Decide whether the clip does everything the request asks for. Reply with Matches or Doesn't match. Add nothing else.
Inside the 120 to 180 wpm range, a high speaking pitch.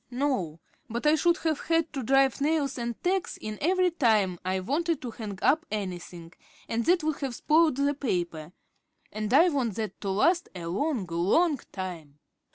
Matches